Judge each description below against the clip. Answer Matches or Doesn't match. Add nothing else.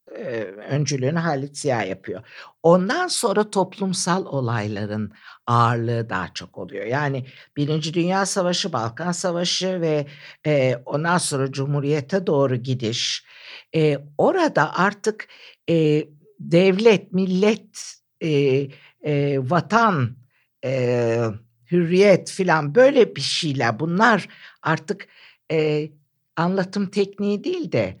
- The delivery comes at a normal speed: Doesn't match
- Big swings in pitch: Matches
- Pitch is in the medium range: Matches